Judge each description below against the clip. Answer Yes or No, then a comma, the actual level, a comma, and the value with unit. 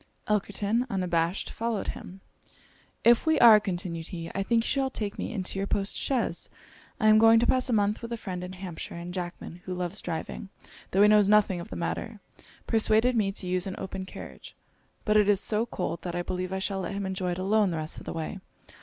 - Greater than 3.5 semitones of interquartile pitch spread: No, average, 3.1 semitones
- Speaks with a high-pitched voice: Yes, high, 195 Hz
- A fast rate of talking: Yes, fast, 225 wpm